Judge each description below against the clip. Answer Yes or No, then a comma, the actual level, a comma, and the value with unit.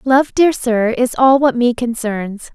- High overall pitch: Yes, high, 245 Hz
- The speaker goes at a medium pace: Yes, average, 190 wpm